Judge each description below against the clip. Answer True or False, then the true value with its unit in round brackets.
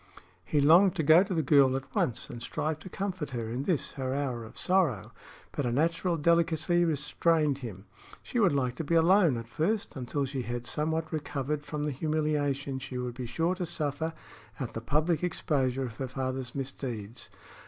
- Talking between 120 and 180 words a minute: False (190 wpm)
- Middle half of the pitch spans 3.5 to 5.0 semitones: True (4.1 semitones)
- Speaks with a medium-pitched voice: True (145 Hz)